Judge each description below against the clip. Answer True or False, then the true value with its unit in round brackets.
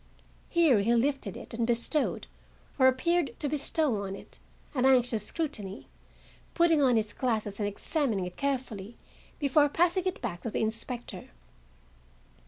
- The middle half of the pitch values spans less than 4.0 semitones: False (5.2 semitones)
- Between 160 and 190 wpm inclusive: False (145 wpm)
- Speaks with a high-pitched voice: True (250 Hz)